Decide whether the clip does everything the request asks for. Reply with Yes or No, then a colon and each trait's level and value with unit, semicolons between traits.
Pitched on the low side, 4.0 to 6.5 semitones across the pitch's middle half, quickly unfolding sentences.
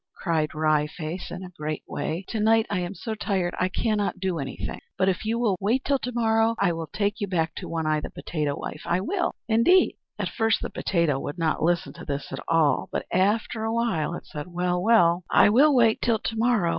No: medium, 185 Hz; average, 5.3 semitones; fast, 230 wpm